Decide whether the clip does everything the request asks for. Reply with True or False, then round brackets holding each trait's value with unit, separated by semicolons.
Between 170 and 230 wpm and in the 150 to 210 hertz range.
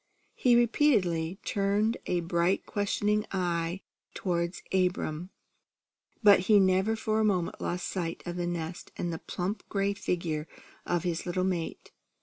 False (140 wpm; 185 Hz)